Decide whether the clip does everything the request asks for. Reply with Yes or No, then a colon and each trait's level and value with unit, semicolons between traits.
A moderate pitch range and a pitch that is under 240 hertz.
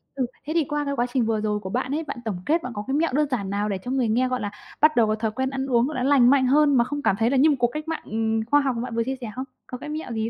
No: average, 4.3 semitones; very high, 255 Hz